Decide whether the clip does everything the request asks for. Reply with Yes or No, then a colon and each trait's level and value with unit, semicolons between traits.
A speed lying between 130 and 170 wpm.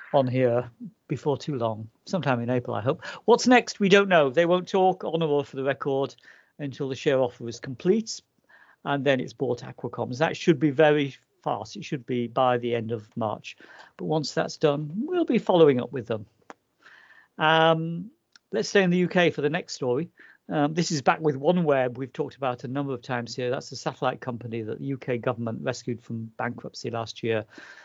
No: fast, 205 wpm